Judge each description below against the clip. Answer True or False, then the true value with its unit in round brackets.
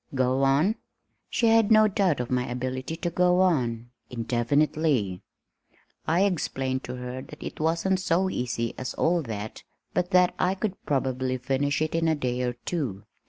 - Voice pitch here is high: False (140 Hz)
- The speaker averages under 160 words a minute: False (165 wpm)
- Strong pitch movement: True (6.1 semitones)